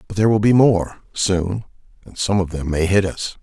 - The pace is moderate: No, fast, 225 wpm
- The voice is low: Yes, very low, 95 Hz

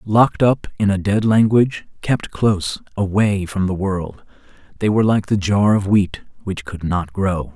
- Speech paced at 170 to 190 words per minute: Yes, average, 185 wpm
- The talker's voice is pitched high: No, low, 100 Hz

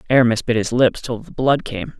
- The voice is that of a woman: No, male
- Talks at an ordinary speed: No, fast, 240 wpm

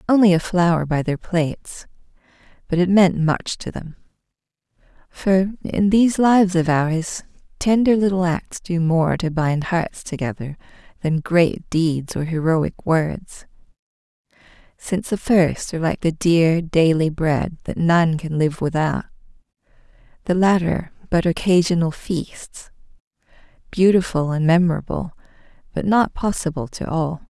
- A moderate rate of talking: No, slow, 130 wpm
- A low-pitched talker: No, medium, 170 Hz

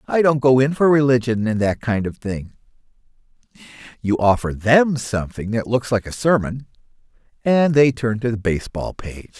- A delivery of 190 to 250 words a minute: No, average, 170 wpm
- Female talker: No, male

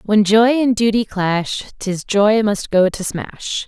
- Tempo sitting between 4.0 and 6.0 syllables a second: No, 3.8 syllables/s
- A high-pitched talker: Yes, high, 205 Hz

